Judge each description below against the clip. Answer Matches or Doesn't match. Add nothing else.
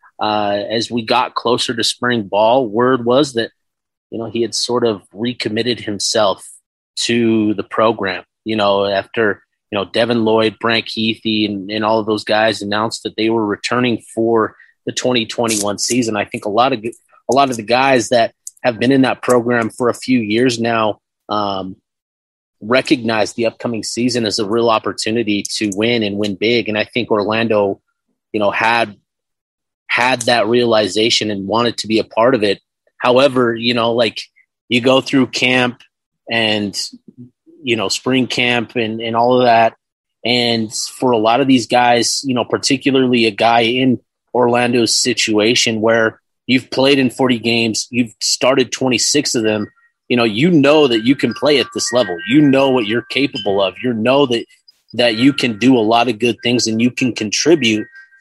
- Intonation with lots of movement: Doesn't match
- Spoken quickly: Doesn't match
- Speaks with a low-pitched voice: Matches